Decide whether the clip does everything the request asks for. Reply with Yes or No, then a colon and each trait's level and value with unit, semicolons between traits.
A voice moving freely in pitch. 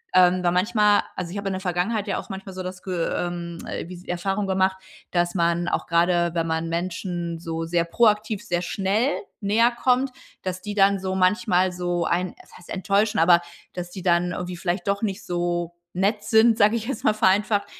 No: average, 2.9 semitones